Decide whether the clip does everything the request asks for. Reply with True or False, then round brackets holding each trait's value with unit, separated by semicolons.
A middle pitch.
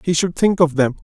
True (165 Hz)